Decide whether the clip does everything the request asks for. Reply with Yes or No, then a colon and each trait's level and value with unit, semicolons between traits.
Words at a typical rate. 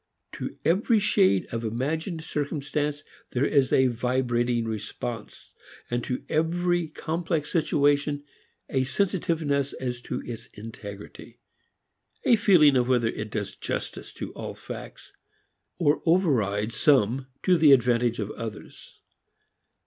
No: slow, 120 wpm